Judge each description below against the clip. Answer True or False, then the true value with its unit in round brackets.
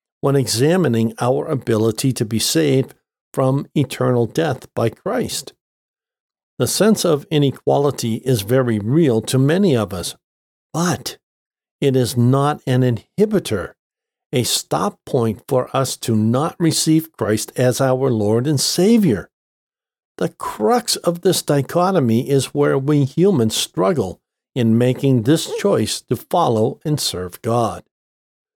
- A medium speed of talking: False (130 wpm)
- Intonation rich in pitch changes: False (5.0 semitones)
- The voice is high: False (130 Hz)